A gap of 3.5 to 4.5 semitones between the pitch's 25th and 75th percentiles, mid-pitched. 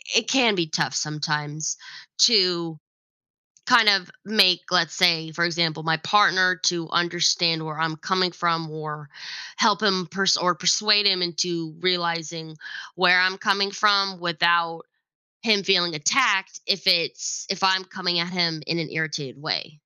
No: average, 2.8 semitones; medium, 175 Hz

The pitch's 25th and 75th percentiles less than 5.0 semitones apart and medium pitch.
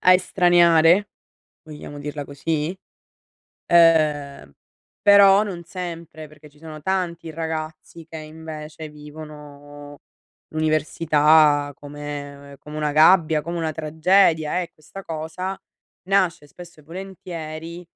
Yes: narrow, 2.4 semitones; medium, 155 Hz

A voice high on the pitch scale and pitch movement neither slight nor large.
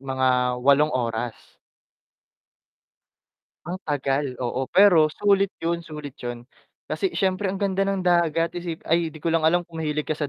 No: medium, 160 Hz; average, 4.5 semitones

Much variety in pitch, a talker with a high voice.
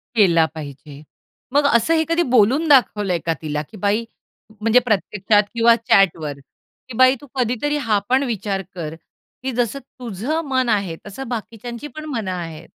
Yes: wide, 5.7 semitones; high, 220 Hz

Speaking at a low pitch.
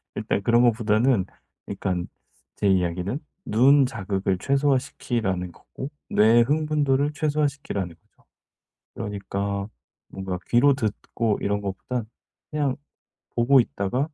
Yes: low, 115 Hz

